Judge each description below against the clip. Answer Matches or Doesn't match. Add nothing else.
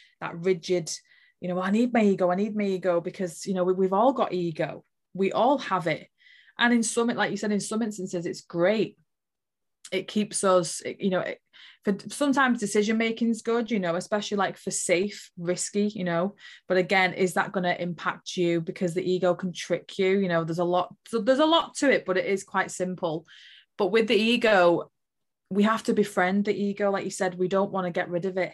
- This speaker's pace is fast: Matches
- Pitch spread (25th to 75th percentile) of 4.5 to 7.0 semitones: Doesn't match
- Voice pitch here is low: Doesn't match